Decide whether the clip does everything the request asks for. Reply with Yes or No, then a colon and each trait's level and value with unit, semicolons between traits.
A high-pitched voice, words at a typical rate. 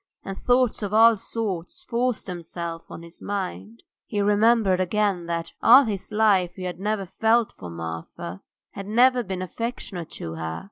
Yes: high, 195 Hz; average, 160 wpm